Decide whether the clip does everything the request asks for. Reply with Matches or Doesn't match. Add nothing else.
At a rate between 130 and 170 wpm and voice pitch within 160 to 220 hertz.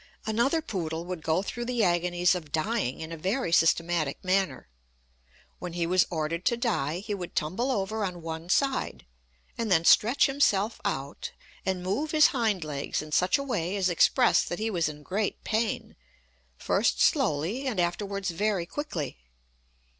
Matches